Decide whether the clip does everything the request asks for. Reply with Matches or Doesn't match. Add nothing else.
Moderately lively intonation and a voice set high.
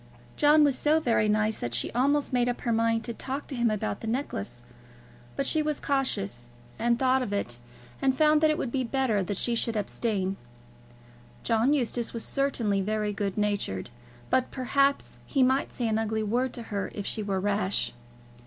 Matches